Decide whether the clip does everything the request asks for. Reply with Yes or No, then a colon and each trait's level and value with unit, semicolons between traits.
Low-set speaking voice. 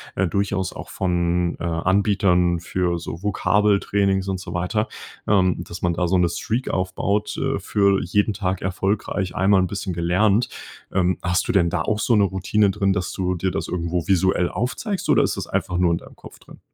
Yes: very low, 95 Hz